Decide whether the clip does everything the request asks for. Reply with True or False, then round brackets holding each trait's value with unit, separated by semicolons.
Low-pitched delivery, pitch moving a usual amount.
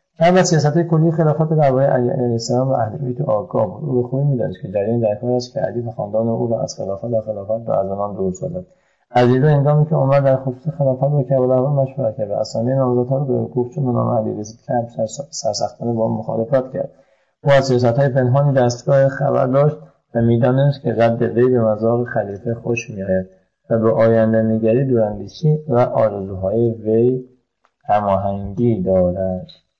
True (125 Hz; 3.5 semitones)